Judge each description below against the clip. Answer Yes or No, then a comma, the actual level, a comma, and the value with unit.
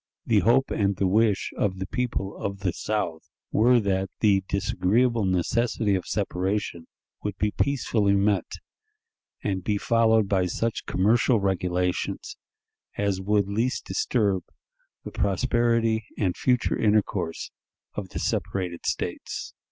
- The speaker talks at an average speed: No, slow, 130 wpm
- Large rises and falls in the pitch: No, average, 3.0 semitones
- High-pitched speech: No, low, 100 Hz